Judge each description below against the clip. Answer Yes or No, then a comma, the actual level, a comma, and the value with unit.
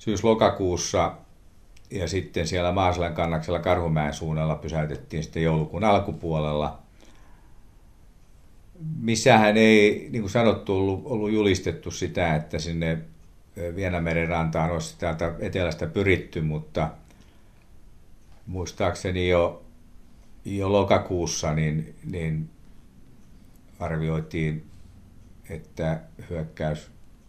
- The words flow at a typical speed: No, slow, 85 wpm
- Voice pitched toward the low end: Yes, very low, 85 Hz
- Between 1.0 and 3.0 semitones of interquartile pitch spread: No, average, 3.6 semitones